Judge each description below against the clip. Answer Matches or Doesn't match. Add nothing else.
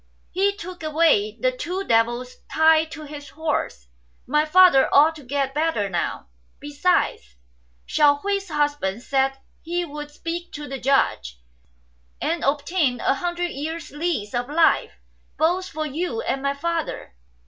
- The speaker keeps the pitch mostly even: Doesn't match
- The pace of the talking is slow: Doesn't match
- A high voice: Matches